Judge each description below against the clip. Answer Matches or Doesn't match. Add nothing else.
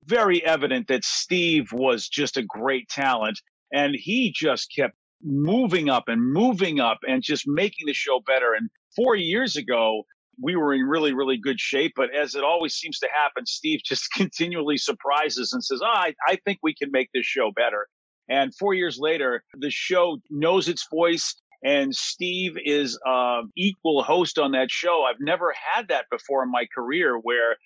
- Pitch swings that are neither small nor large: Doesn't match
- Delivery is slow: Doesn't match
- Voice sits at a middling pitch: Matches